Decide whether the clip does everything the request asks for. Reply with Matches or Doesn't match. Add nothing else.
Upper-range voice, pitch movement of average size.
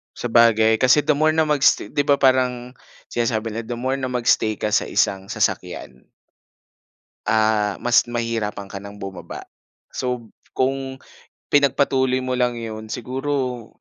Doesn't match